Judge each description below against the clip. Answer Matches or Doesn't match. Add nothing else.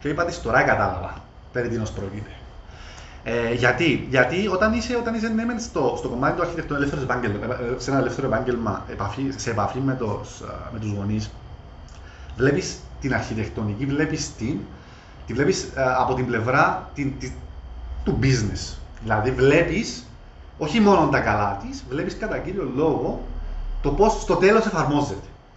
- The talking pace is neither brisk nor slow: Matches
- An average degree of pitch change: Doesn't match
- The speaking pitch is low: Matches